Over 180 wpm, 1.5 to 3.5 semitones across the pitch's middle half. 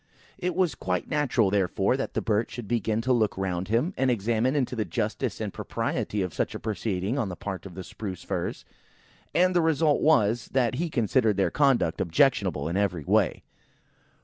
No: average, 195 wpm; wide, 5.6 semitones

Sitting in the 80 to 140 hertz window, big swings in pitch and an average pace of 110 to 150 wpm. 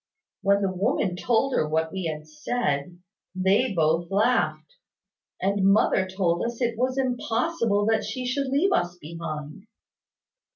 No: high, 195 Hz; wide, 6.1 semitones; average, 140 wpm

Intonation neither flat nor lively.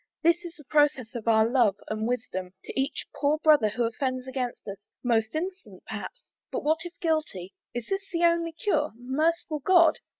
No: wide, 6.2 semitones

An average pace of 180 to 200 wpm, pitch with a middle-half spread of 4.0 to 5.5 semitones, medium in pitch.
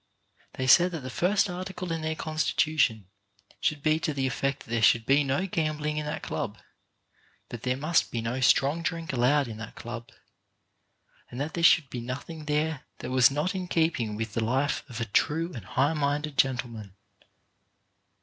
Yes: average, 185 wpm; average, 4.4 semitones; medium, 145 Hz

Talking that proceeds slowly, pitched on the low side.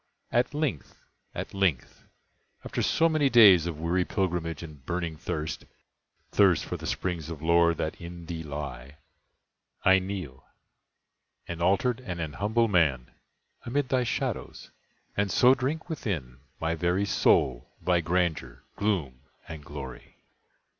Yes: slow, 130 wpm; very low, 85 Hz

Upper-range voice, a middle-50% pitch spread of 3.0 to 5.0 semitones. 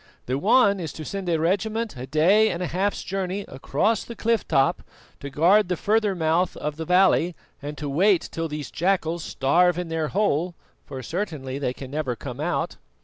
No: medium, 170 Hz; average, 4.7 semitones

